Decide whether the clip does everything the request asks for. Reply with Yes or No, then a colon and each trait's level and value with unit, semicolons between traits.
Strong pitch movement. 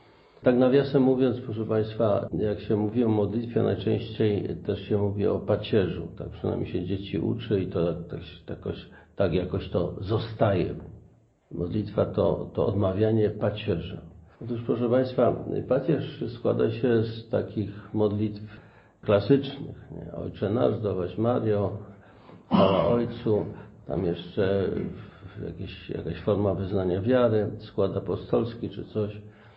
No: average, 2.8 semitones